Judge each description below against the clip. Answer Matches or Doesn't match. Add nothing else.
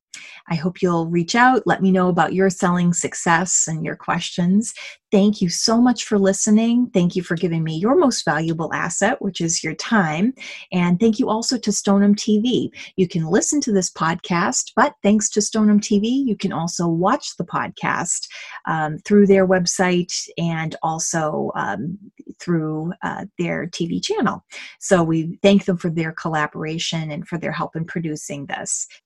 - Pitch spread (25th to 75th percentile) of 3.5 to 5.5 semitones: Matches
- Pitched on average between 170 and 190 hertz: Matches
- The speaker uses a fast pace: Doesn't match